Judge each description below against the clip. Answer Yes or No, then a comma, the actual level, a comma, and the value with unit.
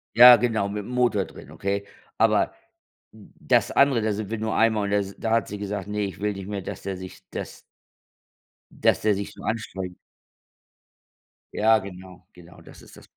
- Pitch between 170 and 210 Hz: No, low, 105 Hz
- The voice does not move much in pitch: Yes, narrow, 2.3 semitones